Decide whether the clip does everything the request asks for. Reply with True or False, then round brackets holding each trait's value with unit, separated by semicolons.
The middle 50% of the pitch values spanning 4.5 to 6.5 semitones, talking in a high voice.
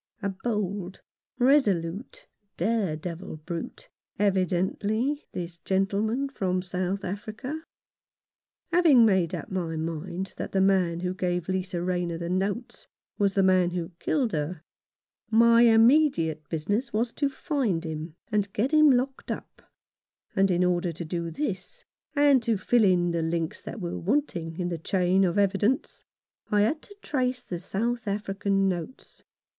True (4.9 semitones; 195 Hz)